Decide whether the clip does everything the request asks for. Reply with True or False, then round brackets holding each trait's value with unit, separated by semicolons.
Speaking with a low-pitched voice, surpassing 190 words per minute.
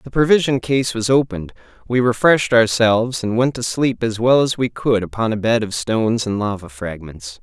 True (115 Hz; 200 wpm)